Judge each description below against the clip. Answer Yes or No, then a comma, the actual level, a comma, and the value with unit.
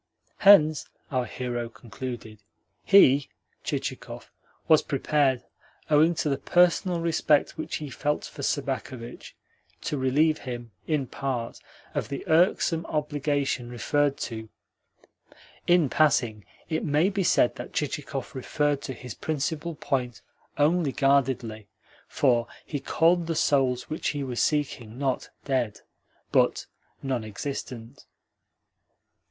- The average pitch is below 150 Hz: Yes, medium, 140 Hz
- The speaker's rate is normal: No, slow, 120 wpm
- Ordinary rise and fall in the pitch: Yes, average, 3.7 semitones